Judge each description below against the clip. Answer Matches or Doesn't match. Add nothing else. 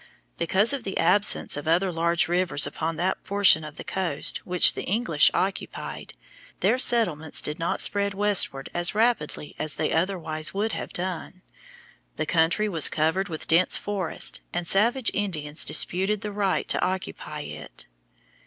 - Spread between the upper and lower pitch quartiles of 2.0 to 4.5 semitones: Matches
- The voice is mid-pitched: Matches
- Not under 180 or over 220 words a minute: Doesn't match